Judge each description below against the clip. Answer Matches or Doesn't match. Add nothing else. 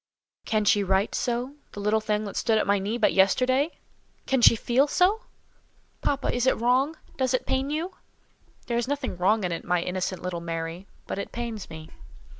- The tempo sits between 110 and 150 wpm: Doesn't match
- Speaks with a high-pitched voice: Matches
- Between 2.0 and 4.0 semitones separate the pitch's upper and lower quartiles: Doesn't match